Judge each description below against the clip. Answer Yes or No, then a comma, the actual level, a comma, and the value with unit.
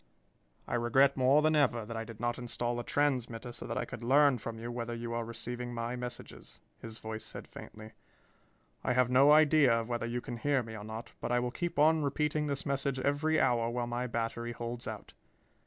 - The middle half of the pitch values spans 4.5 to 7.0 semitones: No, average, 3.0 semitones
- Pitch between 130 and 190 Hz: No, low, 120 Hz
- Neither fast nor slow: No, fast, 215 wpm